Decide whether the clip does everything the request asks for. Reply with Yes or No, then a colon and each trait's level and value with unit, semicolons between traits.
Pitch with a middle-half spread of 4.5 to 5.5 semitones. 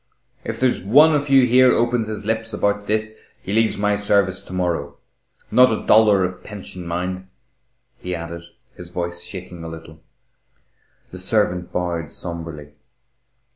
No: average, 4.0 semitones